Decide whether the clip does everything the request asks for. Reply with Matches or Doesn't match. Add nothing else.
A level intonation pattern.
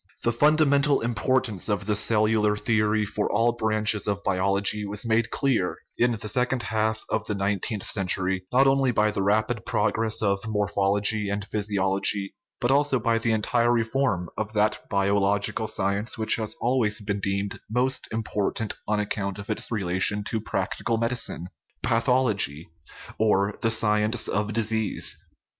Matches